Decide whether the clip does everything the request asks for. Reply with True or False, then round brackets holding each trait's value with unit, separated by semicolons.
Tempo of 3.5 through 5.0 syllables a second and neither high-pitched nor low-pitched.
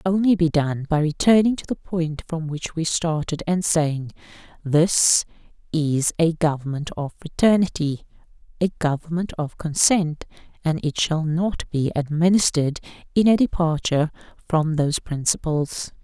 True (4.8 syllables/s; 160 Hz)